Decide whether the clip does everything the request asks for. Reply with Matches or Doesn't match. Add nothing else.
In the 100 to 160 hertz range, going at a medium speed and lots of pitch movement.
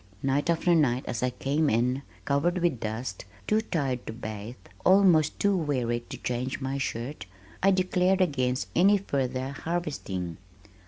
Matches